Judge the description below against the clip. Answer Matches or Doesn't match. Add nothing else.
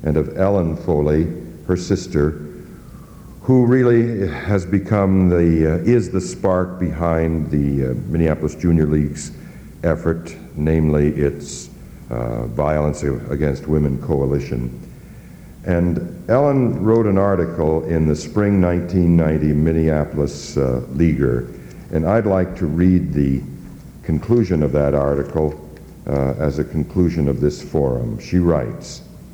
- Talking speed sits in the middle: Doesn't match